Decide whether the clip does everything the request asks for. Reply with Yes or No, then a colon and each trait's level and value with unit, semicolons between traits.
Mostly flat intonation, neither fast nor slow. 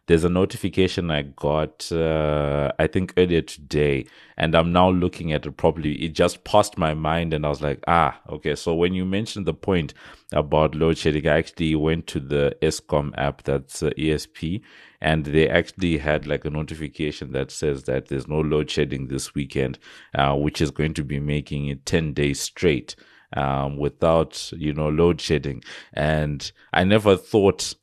Yes: narrow, 2.3 semitones; average, 180 wpm